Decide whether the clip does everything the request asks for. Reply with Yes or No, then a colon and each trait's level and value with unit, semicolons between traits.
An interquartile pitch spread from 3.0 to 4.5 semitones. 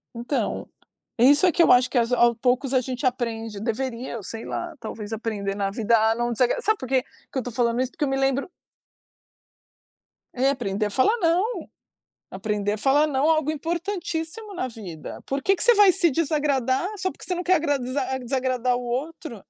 No: wide, 5.4 semitones